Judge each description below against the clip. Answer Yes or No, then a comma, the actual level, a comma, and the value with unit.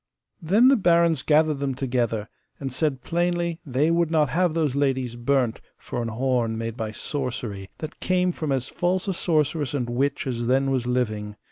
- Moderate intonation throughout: Yes, average, 5.0 semitones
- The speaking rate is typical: Yes, average, 180 wpm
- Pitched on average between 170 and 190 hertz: No, low, 135 Hz